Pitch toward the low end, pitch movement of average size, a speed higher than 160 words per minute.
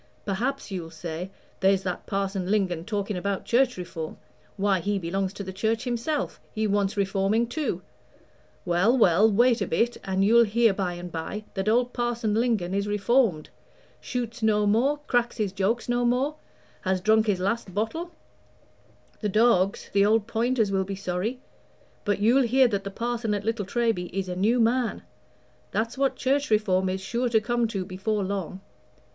No: high, 210 Hz; average, 3.7 semitones; average, 175 wpm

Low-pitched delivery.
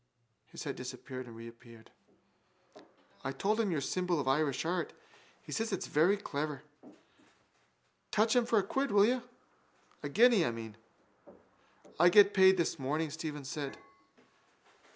No: medium, 160 Hz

